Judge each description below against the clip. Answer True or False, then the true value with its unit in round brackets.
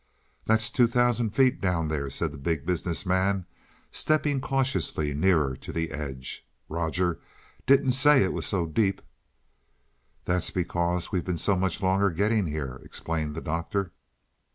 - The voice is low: True (90 Hz)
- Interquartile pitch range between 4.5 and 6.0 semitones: True (4.9 semitones)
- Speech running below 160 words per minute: True (150 wpm)